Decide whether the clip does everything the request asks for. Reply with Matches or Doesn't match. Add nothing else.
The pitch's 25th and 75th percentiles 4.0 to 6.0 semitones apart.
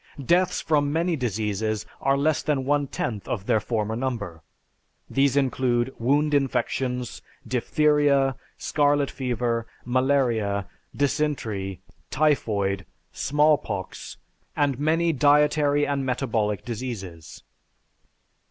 Matches